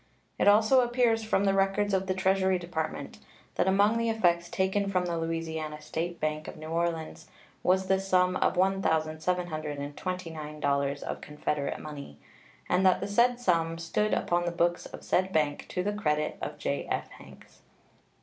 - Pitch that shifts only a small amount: No, average, 3.5 semitones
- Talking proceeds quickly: No, average, 160 wpm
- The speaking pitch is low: No, medium, 180 Hz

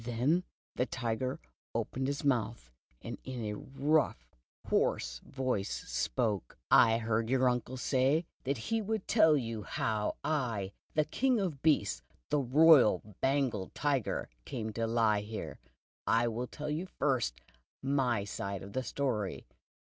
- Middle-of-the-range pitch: No, low, 125 Hz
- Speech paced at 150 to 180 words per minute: No, average, 140 wpm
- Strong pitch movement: No, average, 4.5 semitones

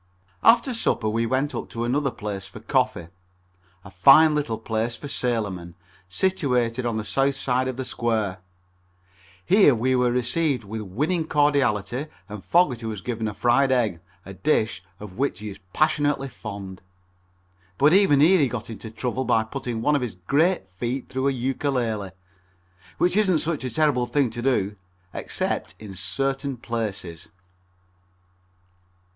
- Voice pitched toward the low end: Yes, low, 125 Hz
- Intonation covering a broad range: No, average, 4.5 semitones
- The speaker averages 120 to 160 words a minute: Yes, average, 155 wpm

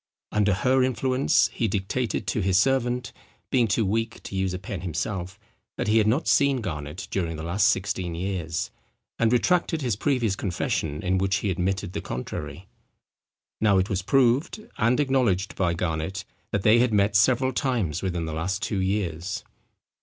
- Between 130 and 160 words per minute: No, average, 170 wpm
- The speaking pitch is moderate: No, low, 100 Hz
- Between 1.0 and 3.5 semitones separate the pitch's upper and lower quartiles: No, average, 4.7 semitones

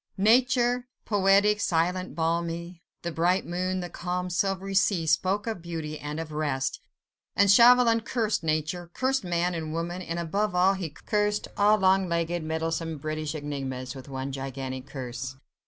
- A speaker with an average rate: Yes, average, 155 wpm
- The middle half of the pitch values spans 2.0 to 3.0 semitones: No, average, 3.9 semitones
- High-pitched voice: No, medium, 170 Hz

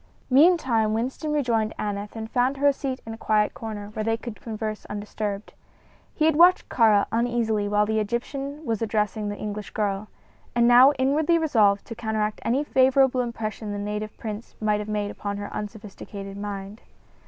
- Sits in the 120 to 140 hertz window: No, high, 220 Hz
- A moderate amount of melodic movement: Yes, average, 3.2 semitones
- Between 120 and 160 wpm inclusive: No, average, 175 wpm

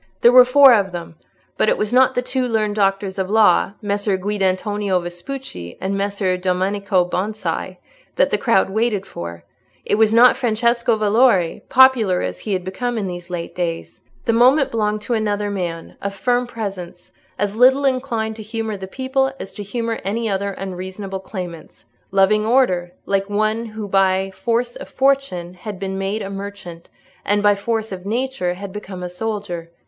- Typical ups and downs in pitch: Yes, average, 3.5 semitones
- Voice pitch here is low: No, high, 205 Hz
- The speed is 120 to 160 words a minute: No, average, 175 wpm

